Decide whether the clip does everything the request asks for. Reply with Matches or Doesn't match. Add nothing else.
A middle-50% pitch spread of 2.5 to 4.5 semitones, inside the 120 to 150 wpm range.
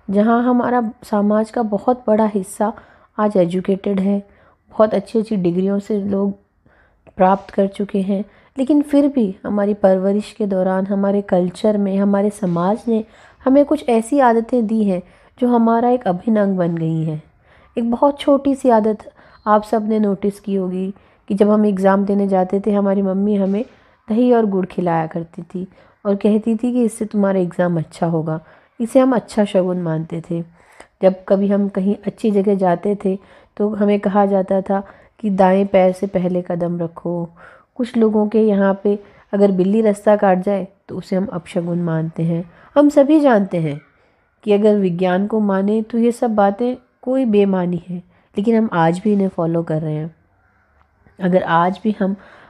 Doesn't match